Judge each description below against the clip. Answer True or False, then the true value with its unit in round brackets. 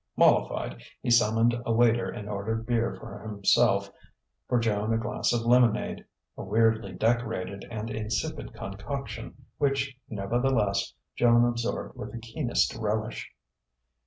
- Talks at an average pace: False (130 wpm)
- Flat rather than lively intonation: True (2.0 semitones)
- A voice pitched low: True (115 Hz)